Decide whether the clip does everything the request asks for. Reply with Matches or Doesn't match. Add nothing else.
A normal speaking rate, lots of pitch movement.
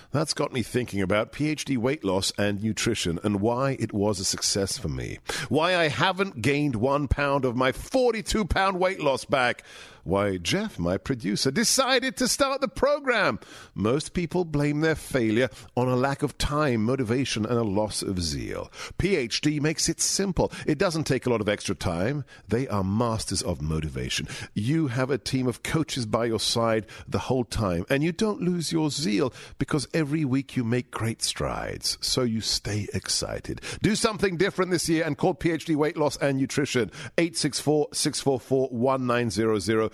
Matches